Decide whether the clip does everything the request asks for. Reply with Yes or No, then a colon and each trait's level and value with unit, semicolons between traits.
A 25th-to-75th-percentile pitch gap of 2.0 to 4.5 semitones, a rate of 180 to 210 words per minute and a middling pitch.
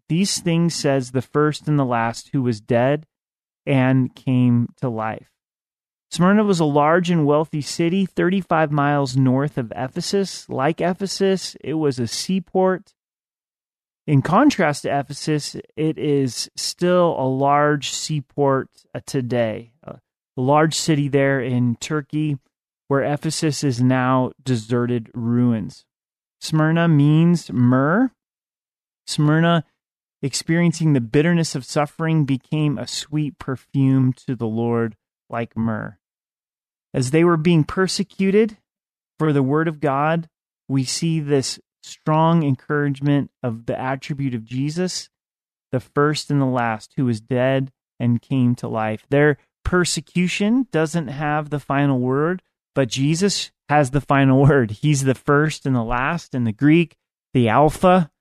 No: average, 3.8 semitones; slow, 135 wpm; medium, 145 Hz